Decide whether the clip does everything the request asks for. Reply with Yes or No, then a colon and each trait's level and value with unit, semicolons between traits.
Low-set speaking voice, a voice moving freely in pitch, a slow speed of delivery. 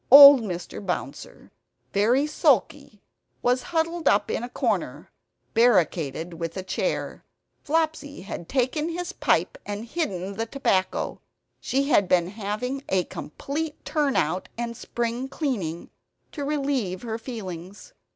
No: high, 235 Hz; wide, 7.1 semitones; slow, 130 wpm